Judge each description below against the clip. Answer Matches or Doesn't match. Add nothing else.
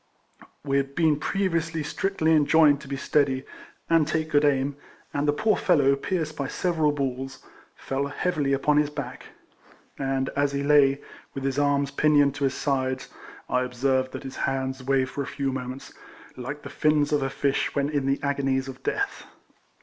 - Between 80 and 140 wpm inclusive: Doesn't match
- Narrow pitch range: Matches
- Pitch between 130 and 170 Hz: Matches